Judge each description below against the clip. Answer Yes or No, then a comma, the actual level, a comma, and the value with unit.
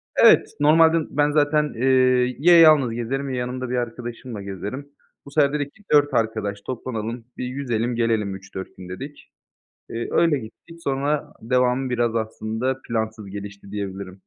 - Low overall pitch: Yes, low, 125 Hz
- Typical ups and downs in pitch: Yes, average, 4.2 semitones